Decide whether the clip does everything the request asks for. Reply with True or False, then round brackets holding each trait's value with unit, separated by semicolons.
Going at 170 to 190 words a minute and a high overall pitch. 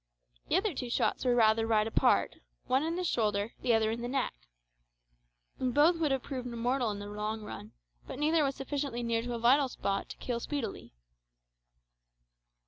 True (180 wpm; 245 Hz)